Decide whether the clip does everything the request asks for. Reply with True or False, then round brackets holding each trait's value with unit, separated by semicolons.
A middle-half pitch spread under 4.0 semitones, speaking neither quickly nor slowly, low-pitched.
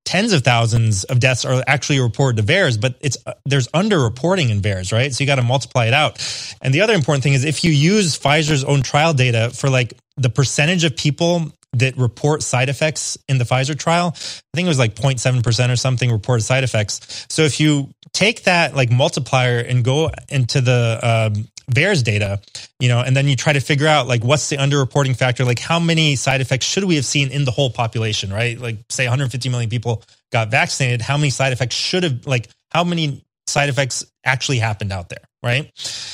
False (3.4 semitones; 215 wpm; 130 Hz)